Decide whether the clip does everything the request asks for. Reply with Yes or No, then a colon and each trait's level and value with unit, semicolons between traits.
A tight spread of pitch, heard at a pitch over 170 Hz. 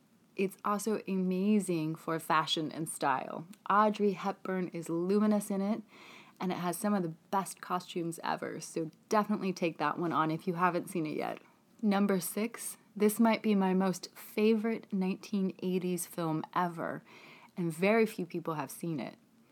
No: average, 3.5 semitones; high, 190 Hz